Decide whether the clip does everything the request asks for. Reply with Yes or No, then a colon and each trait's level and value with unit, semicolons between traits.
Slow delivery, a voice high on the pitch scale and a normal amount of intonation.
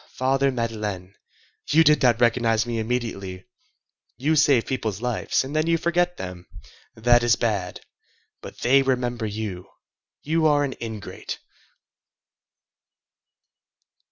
No: slow, 120 wpm; low, 120 Hz; average, 4.0 semitones